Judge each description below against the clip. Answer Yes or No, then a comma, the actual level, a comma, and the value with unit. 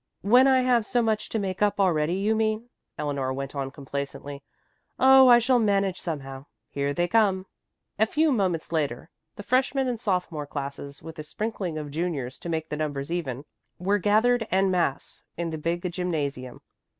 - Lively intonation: Yes, wide, 6.9 semitones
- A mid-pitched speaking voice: Yes, medium, 175 Hz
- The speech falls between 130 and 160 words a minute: No, average, 175 wpm